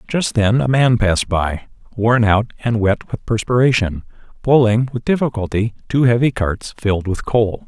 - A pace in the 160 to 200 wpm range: Yes, average, 165 wpm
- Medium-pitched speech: No, low, 115 Hz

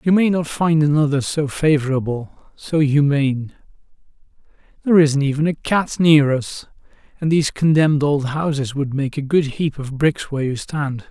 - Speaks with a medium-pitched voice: Yes, medium, 145 Hz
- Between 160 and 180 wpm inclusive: Yes, average, 165 wpm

